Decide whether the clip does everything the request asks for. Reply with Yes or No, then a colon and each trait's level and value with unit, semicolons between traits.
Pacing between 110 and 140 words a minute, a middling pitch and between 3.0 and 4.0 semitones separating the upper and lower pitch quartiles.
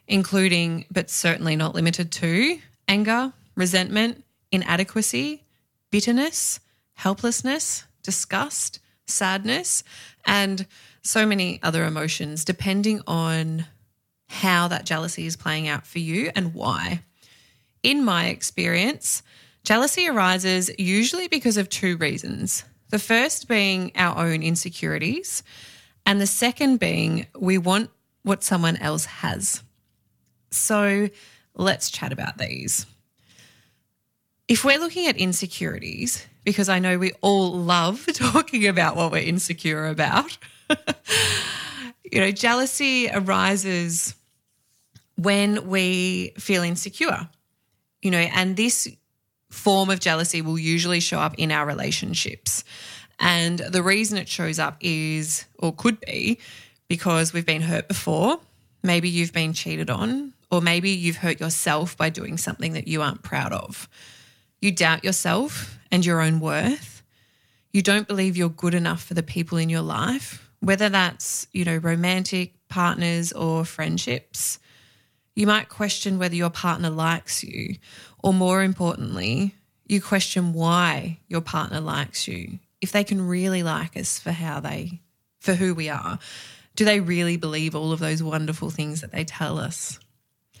Yes: slow, 135 wpm; medium, 180 Hz; average, 3.6 semitones